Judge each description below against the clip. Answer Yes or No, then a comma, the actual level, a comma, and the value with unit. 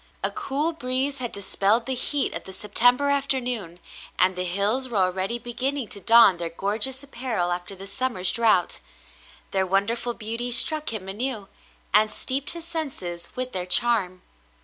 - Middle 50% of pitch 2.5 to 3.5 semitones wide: No, average, 5.3 semitones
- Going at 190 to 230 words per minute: No, average, 160 wpm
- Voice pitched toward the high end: Yes, high, 230 Hz